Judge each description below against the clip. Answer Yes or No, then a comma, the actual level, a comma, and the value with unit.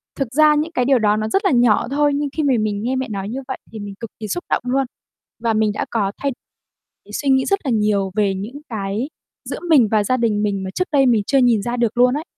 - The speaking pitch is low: No, high, 240 Hz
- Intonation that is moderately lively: Yes, average, 4.5 semitones